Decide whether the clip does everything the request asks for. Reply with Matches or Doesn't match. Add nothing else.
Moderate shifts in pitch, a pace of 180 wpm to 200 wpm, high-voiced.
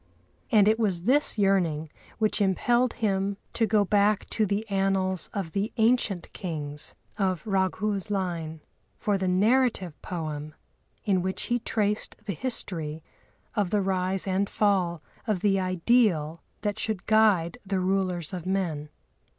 Doesn't match